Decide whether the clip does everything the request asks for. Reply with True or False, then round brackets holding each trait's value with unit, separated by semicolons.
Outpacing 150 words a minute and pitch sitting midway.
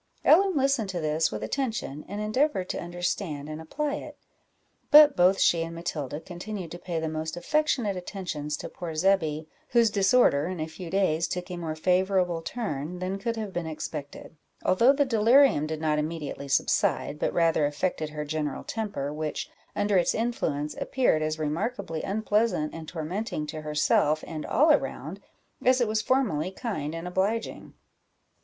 True (165 wpm; 175 Hz)